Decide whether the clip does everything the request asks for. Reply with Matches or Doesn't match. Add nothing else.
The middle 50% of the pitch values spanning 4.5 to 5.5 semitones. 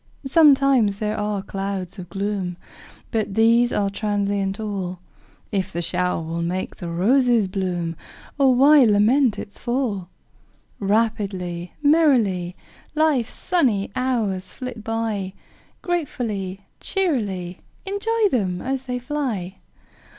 Matches